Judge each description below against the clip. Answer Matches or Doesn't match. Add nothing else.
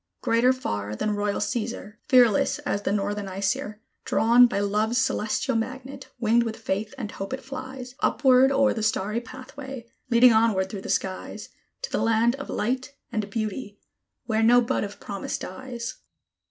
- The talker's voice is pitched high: Matches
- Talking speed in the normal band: Matches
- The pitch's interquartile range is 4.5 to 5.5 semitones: Doesn't match